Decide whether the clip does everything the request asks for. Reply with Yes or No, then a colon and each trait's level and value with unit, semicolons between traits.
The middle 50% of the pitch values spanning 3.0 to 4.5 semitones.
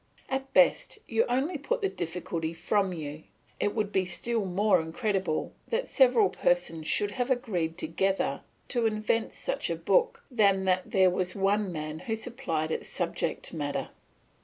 No: wide, 5.6 semitones